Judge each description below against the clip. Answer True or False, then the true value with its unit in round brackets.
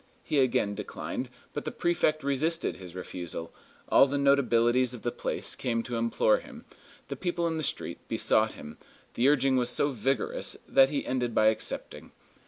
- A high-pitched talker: False (130 Hz)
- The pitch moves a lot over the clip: False (3.8 semitones)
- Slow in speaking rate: False (175 wpm)